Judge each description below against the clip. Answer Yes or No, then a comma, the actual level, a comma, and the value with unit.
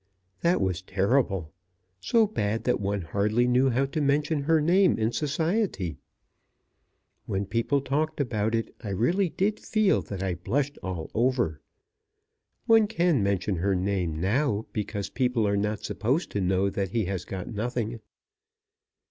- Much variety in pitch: Yes, wide, 6.7 semitones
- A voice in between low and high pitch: No, low, 115 Hz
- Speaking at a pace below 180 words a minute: Yes, average, 150 wpm